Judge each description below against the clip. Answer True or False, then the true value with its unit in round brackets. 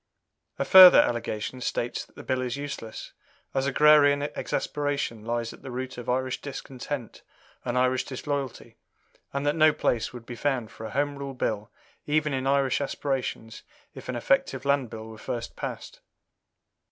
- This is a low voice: True (130 Hz)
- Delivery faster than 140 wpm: True (165 wpm)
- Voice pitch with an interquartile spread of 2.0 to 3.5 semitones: True (3.0 semitones)